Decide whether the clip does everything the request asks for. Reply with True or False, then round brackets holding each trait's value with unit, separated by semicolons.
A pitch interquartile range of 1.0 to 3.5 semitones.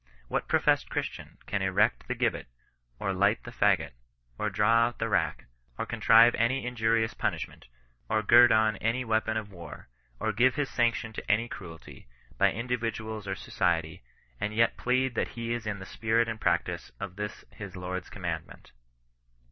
True (2.8 semitones)